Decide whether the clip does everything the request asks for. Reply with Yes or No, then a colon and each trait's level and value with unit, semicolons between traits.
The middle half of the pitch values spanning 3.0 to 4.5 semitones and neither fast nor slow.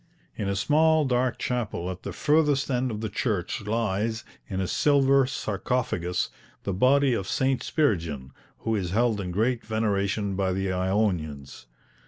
No: average, 5.2 semitones; average, 155 wpm